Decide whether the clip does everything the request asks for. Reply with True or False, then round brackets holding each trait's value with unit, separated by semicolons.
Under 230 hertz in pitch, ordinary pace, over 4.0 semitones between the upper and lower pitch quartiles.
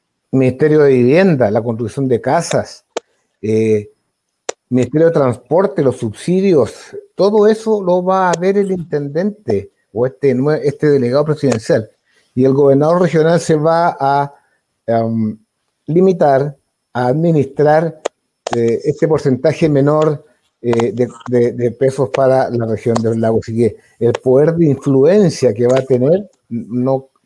True (135 Hz; 135 wpm; 5.1 semitones)